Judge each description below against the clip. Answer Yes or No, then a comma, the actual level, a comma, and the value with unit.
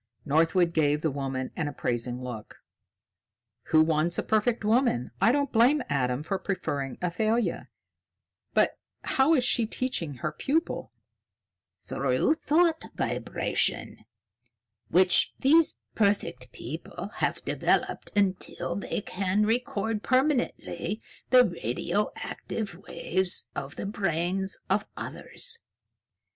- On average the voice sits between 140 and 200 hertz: Yes, high, 190 Hz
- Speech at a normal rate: No, slow, 110 wpm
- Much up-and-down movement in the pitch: Yes, wide, 7.8 semitones